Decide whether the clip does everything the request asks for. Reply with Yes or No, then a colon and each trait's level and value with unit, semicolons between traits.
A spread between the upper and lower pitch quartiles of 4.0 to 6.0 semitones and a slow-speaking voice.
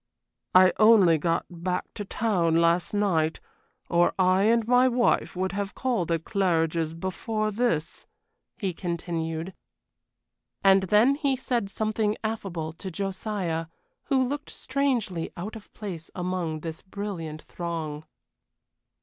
Yes: average, 4.5 semitones; slow, 125 wpm